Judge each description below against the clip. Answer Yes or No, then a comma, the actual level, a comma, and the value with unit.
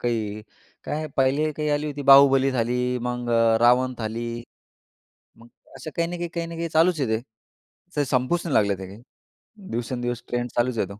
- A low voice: Yes, low, 125 Hz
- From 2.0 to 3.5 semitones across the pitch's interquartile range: No, average, 4.5 semitones